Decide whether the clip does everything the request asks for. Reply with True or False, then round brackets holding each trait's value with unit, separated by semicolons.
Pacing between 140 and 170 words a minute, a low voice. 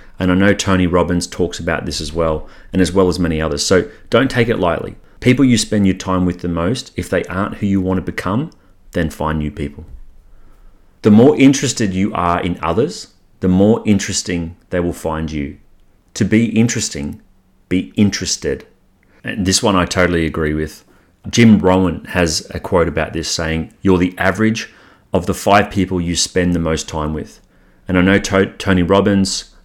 False (190 wpm; 90 Hz)